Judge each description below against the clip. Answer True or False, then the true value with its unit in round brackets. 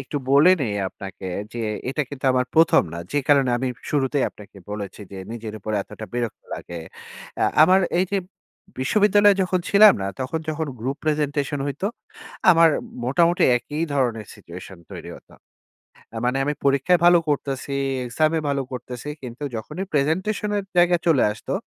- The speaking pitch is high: False (140 Hz)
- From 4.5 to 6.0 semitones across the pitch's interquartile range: True (5.3 semitones)